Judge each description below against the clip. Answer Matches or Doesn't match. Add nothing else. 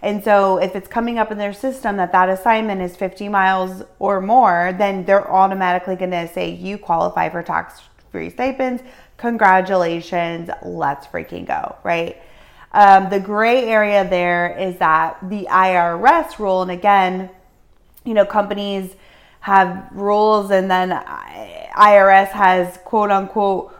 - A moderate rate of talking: Matches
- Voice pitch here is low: Doesn't match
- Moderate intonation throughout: Doesn't match